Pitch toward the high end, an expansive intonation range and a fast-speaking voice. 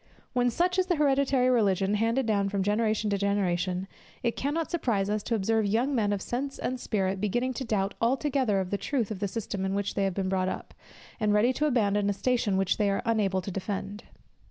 No: high, 210 Hz; average, 4.0 semitones; fast, 220 wpm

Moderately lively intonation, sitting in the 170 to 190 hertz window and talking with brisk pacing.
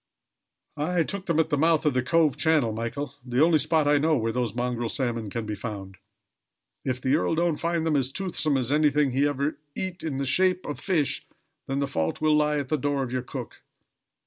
No: average, 4.1 semitones; medium, 145 Hz; fast, 220 wpm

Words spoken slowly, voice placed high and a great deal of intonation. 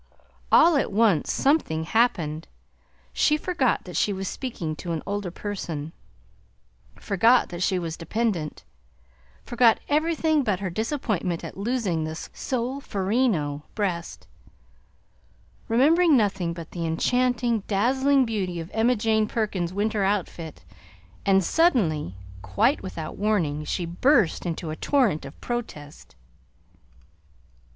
Yes: slow, 120 wpm; high, 200 Hz; wide, 6.5 semitones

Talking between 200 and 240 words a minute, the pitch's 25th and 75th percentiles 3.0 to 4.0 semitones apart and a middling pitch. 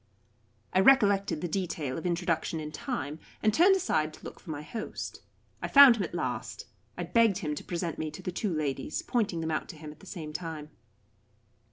No: fast, 205 wpm; average, 4.6 semitones; medium, 170 Hz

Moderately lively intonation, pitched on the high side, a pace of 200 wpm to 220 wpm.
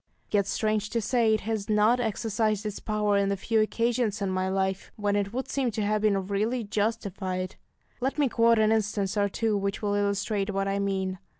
No: narrow, 2.0 semitones; high, 210 Hz; fast, 205 wpm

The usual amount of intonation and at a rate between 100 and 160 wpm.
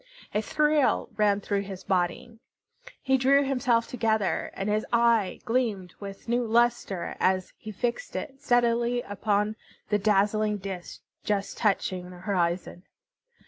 Yes: average, 3.5 semitones; slow, 135 wpm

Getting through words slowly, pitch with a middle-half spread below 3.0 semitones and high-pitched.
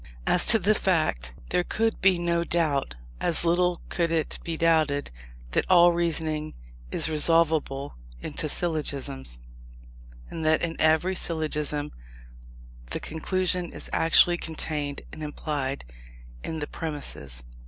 No: slow, 125 wpm; narrow, 2.5 semitones; medium, 160 Hz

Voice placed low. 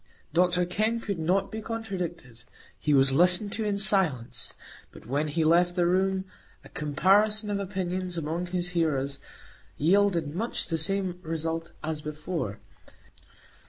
No: medium, 175 Hz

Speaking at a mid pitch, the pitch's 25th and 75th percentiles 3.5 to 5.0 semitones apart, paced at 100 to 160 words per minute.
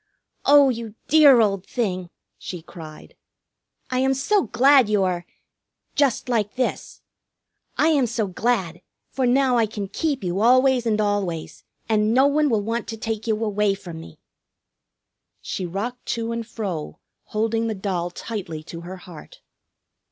No: high, 220 Hz; average, 4.7 semitones; average, 155 wpm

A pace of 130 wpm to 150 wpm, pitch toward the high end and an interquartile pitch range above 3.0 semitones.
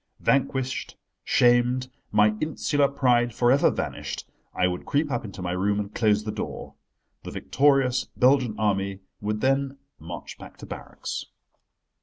No: average, 145 wpm; low, 120 Hz; average, 4.5 semitones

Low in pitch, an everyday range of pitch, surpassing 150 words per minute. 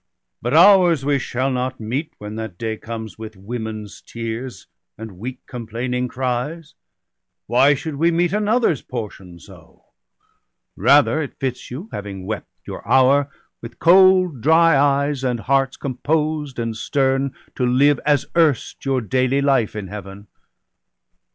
No: low, 130 Hz; average, 4.4 semitones; average, 145 wpm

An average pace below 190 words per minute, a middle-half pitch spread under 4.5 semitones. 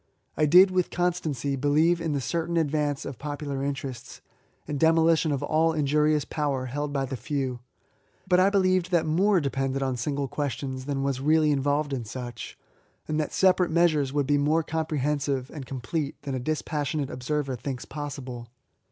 Yes: average, 175 wpm; average, 2.9 semitones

